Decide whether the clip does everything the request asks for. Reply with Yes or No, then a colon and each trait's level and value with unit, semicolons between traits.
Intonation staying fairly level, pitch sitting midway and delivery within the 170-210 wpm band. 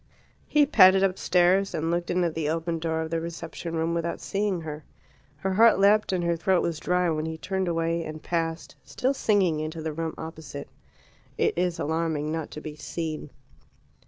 Yes: narrow, 2.2 semitones; medium, 165 Hz; average, 190 wpm